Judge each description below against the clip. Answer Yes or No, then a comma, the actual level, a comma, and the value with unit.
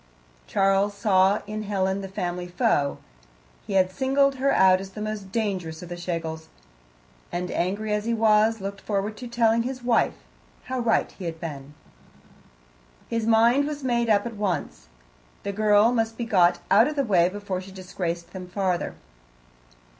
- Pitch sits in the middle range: No, high, 200 Hz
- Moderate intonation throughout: Yes, average, 3.6 semitones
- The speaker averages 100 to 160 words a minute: No, average, 170 wpm